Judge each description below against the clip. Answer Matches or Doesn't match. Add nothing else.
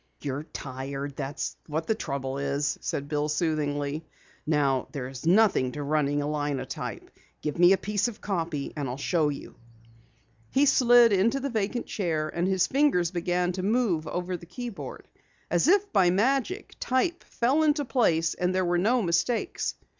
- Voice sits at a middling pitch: Matches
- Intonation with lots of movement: Matches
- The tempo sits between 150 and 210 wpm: Matches